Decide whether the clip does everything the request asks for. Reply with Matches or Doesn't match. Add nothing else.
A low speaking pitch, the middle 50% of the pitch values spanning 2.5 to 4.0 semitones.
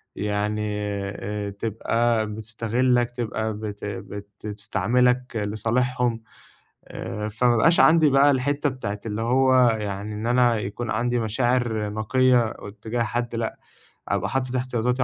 Matches